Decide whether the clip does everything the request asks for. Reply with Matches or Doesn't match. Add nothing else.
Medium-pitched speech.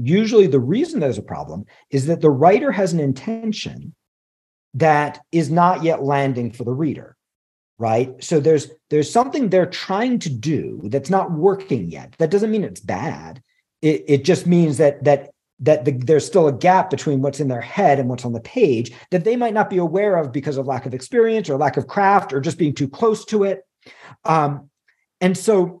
Matches